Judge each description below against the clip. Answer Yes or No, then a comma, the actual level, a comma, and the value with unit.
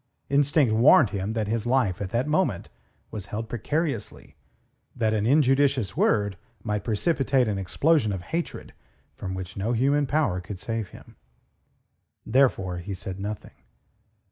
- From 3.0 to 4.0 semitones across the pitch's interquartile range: No, wide, 5.6 semitones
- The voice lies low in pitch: Yes, low, 110 Hz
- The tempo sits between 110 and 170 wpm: Yes, average, 145 wpm